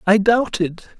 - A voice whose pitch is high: Yes, high, 205 Hz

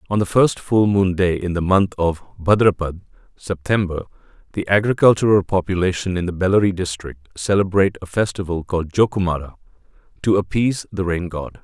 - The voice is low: Yes, very low, 95 Hz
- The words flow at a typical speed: Yes, average, 150 wpm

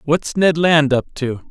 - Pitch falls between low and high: Yes, medium, 150 Hz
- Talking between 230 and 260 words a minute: No, average, 200 wpm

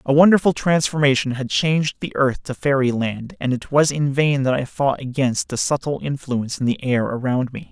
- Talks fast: Yes, fast, 210 wpm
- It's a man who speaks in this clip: Yes, male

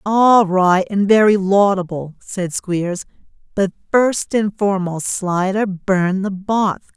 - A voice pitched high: Yes, high, 195 Hz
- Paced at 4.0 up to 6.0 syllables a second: No, 3.5 syllables/s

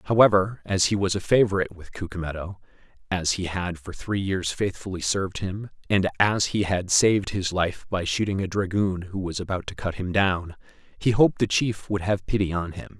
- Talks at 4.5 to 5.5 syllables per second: Yes, 5.3 syllables/s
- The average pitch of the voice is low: Yes, very low, 95 Hz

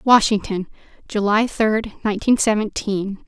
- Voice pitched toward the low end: No, high, 210 Hz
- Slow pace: Yes, slow, 90 wpm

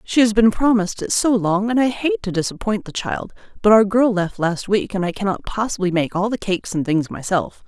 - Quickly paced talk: Yes, fast, 240 wpm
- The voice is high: Yes, high, 200 Hz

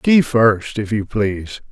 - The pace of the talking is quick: No, average, 175 wpm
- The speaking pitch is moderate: No, low, 110 Hz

